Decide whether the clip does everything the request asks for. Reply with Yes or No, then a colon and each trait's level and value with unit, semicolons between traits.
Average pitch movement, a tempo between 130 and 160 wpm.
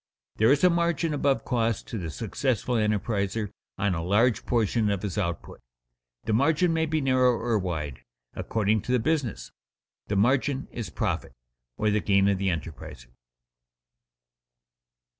Yes: average, 4.8 semitones; average, 150 wpm